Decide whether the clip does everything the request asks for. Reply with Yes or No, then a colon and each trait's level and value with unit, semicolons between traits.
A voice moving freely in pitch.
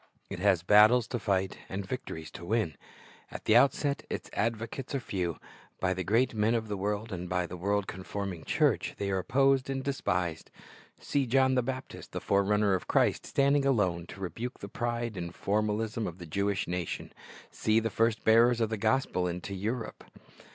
No: average, 4.1 semitones